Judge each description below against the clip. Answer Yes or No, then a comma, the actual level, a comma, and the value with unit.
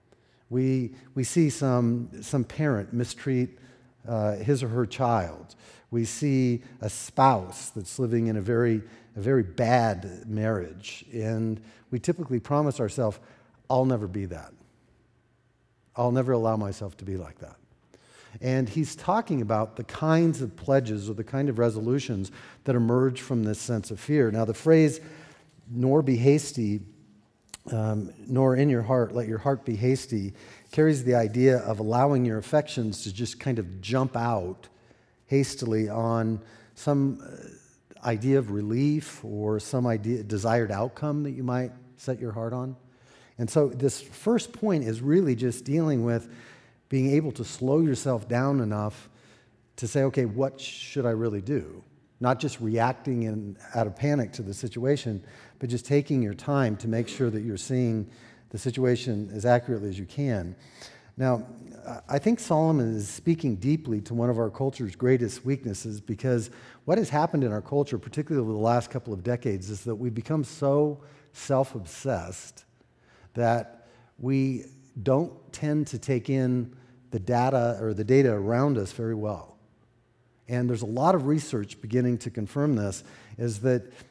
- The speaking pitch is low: Yes, low, 120 Hz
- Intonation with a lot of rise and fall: No, average, 3.1 semitones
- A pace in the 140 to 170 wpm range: Yes, average, 160 wpm